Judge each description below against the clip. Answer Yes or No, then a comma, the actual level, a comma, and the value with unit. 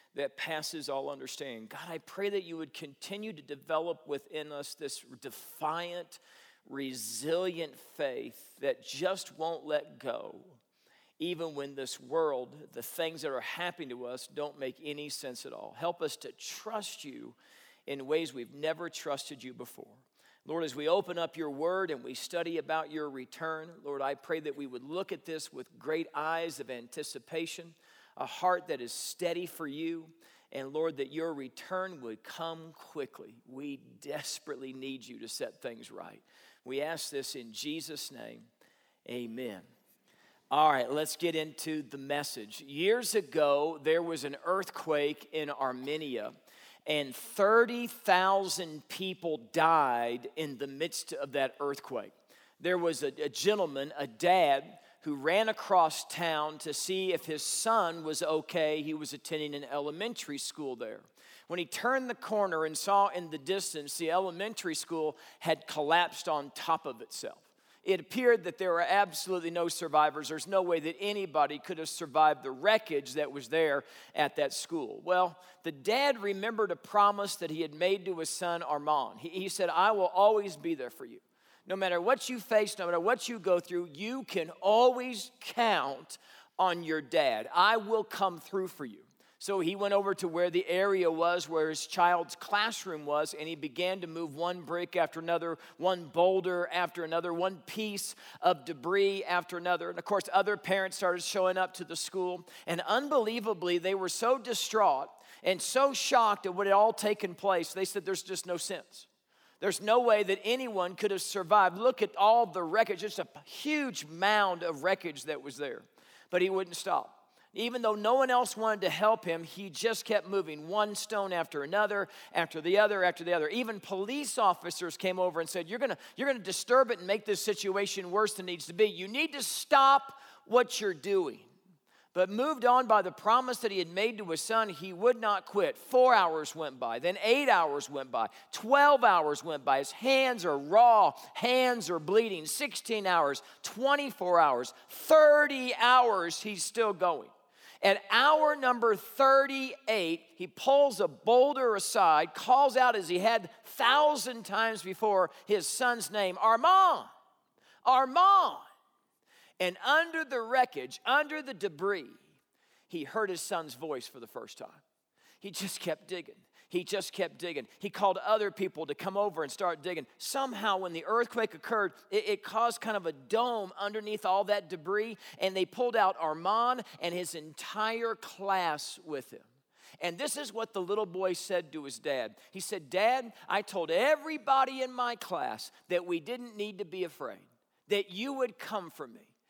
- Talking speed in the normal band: Yes, average, 175 wpm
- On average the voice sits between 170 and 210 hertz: Yes, medium, 185 Hz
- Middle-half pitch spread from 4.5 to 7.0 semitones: Yes, average, 5.3 semitones